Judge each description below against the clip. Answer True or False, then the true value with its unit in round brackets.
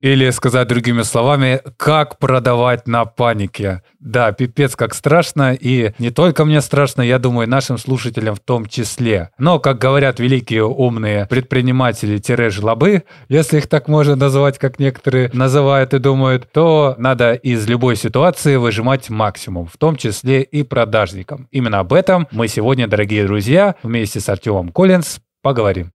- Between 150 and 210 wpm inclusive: True (155 wpm)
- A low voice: True (130 Hz)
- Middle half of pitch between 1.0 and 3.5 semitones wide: True (3.2 semitones)